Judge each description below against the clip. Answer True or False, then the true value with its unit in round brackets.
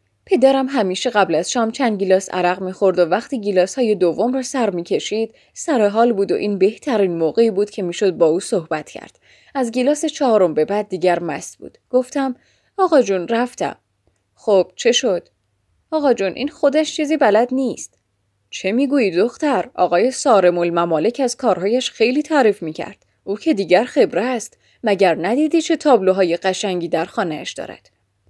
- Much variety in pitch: True (6.3 semitones)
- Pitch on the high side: True (210 Hz)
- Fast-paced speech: True (165 wpm)